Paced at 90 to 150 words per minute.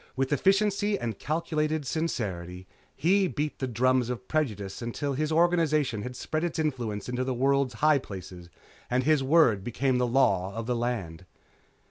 No: average, 160 wpm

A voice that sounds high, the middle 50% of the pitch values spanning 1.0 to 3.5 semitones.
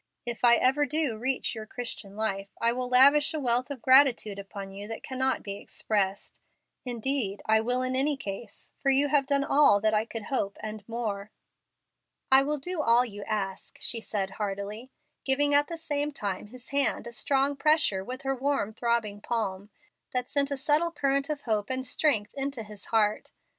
No: high, 245 Hz; average, 4.7 semitones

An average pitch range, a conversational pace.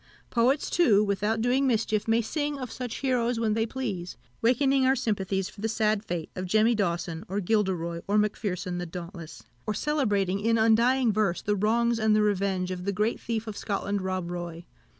Yes: average, 3.6 semitones; average, 190 wpm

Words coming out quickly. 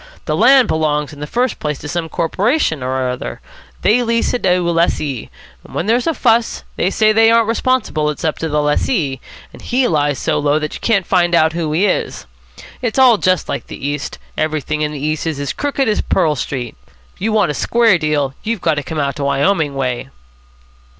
Yes: fast, 210 wpm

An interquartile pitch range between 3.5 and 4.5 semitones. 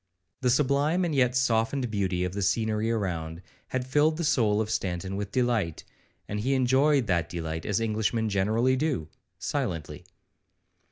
No: average, 5.2 semitones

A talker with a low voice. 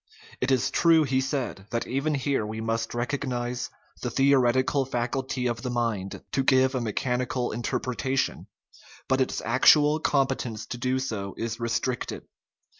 Yes: low, 125 Hz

